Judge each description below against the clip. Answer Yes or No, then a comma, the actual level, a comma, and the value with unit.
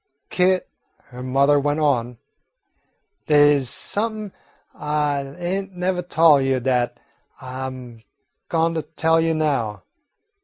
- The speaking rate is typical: No, slow, 120 wpm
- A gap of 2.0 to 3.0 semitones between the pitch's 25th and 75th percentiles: No, average, 4.0 semitones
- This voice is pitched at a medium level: Yes, medium, 145 Hz